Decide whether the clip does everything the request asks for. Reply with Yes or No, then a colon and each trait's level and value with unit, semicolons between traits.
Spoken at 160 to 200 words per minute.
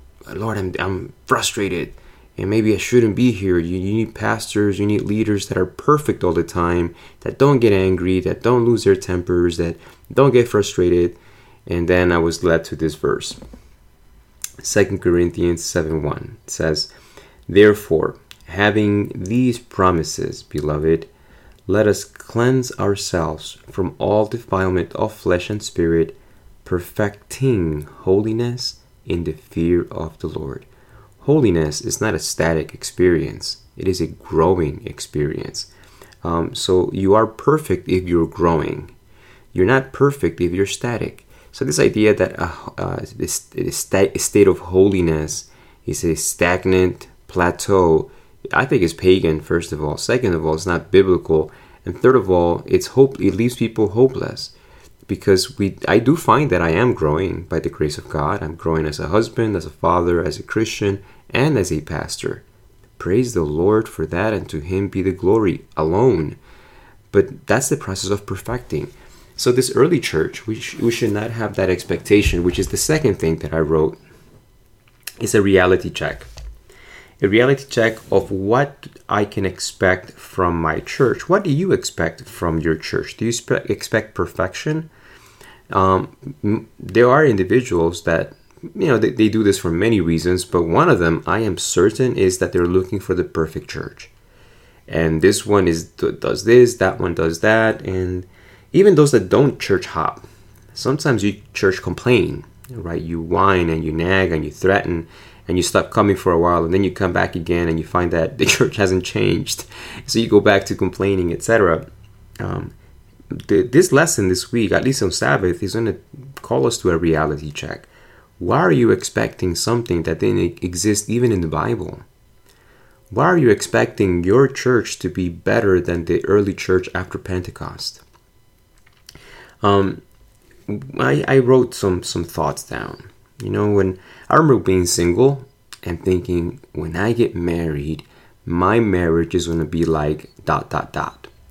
Yes: average, 165 wpm